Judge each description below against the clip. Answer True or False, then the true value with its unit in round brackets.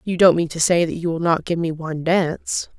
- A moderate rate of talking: False (280 wpm)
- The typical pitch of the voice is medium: True (170 Hz)